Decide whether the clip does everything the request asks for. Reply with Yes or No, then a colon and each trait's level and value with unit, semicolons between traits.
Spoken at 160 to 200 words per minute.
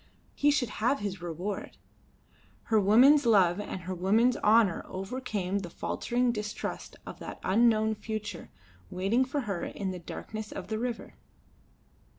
No: average, 145 wpm